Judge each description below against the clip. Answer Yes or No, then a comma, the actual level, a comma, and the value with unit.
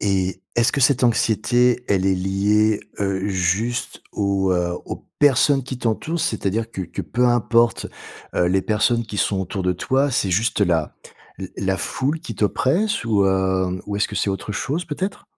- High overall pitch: No, low, 105 Hz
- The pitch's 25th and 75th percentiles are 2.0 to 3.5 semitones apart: No, average, 4.3 semitones